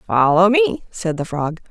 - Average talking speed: Yes, average, 175 wpm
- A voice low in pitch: No, medium, 185 Hz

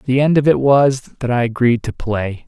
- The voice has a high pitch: No, low, 125 Hz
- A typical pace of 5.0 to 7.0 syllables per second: No, 4.5 syllables/s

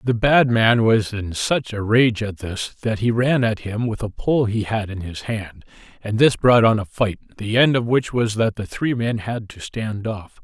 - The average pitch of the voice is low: Yes, low, 110 Hz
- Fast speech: Yes, fast, 240 wpm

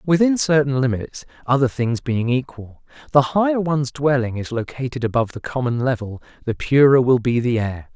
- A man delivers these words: Yes, male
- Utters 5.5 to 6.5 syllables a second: No, 5.3 syllables/s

